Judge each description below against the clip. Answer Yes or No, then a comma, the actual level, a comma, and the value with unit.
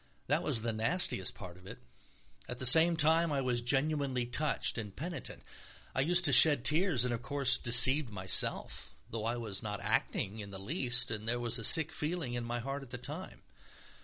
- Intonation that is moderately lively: Yes, average, 4.6 semitones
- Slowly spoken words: No, average, 200 wpm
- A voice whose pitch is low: Yes, low, 125 Hz